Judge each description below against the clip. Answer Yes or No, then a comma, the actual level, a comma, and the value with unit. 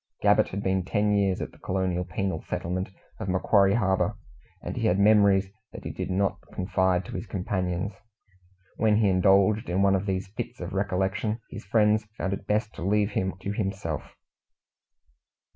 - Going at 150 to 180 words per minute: Yes, average, 175 wpm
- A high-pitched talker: No, very low, 95 Hz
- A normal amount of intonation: No, narrow, 1.8 semitones